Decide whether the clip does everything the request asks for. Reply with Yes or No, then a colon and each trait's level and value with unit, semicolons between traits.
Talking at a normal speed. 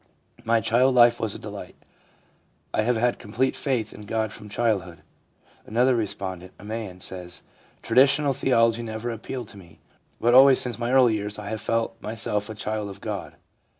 Yes: average, 180 wpm